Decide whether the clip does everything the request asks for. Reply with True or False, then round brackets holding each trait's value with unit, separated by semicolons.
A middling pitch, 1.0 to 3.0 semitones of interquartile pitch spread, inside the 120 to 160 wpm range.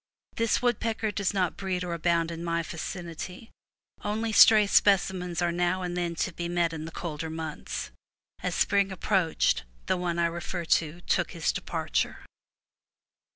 True (175 Hz; 2.4 semitones; 155 wpm)